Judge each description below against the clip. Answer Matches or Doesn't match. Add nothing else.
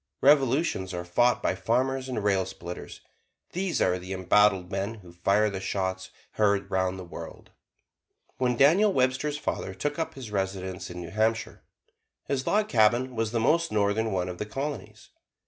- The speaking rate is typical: Matches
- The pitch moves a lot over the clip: Matches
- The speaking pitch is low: Matches